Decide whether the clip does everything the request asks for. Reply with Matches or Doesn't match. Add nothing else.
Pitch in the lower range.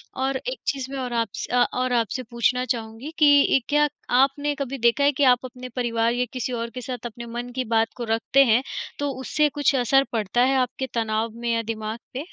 Doesn't match